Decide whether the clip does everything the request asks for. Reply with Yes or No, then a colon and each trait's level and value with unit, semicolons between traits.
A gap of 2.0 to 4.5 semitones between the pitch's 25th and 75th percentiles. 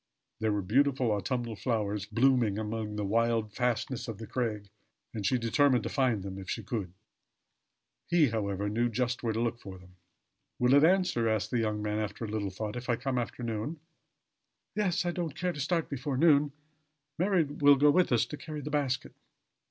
No: average, 4.9 semitones